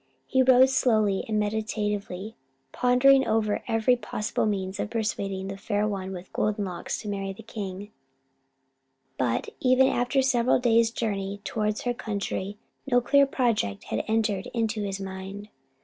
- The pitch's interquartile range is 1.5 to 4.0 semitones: Yes, average, 3.4 semitones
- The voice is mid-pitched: No, high, 215 Hz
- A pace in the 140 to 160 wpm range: Yes, average, 150 wpm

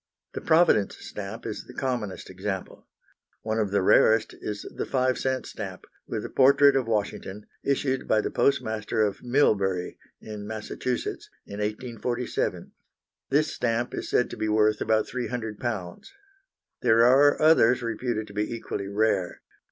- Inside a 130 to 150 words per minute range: Yes, average, 145 wpm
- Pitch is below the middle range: Yes, low, 110 Hz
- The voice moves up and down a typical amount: Yes, average, 3.4 semitones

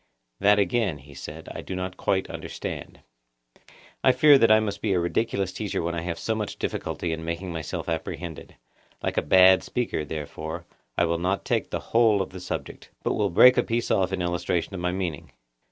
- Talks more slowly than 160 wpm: No, average, 200 wpm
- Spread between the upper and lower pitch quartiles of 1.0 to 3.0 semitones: No, average, 3.4 semitones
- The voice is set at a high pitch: No, very low, 90 Hz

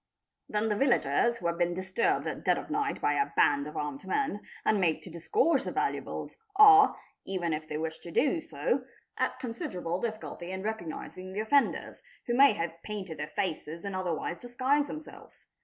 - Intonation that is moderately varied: No, wide, 6.1 semitones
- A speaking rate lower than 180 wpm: No, average, 185 wpm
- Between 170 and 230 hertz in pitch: Yes, high, 190 Hz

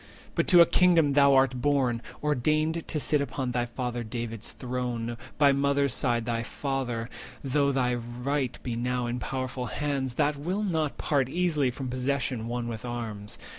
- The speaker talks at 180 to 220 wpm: No, average, 165 wpm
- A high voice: No, low, 130 Hz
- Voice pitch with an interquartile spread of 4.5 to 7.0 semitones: No, average, 3.0 semitones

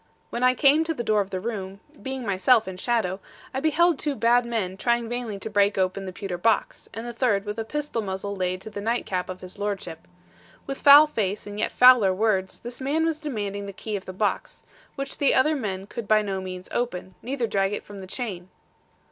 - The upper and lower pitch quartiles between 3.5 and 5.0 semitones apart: Yes, average, 4.4 semitones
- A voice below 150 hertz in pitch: No, high, 215 Hz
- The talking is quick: Yes, fast, 225 wpm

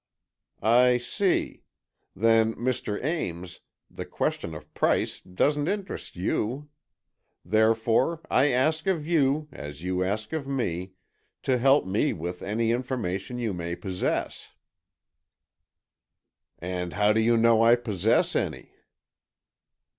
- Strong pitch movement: Yes, wide, 6.4 semitones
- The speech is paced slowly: Yes, slow, 115 wpm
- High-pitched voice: No, low, 115 Hz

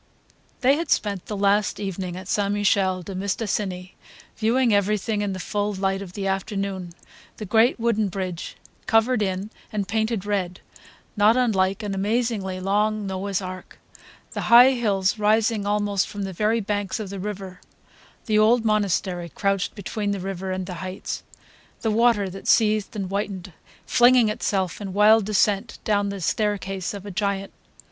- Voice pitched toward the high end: Yes, high, 200 Hz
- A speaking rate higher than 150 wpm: Yes, average, 160 wpm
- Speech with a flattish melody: Yes, narrow, 2.0 semitones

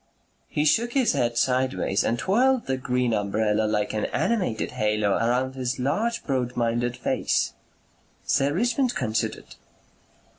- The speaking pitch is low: Yes, low, 125 Hz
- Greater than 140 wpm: No, slow, 135 wpm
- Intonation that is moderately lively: No, wide, 6.1 semitones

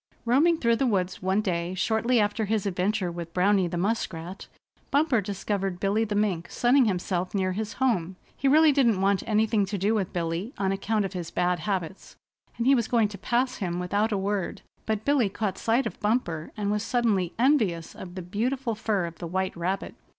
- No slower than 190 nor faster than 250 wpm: Yes, average, 200 wpm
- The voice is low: No, high, 205 Hz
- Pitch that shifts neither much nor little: Yes, average, 3.7 semitones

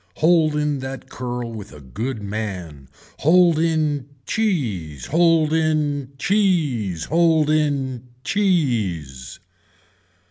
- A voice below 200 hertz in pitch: Yes, medium, 140 Hz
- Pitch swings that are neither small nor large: No, wide, 6.9 semitones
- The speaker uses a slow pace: Yes, slow, 100 wpm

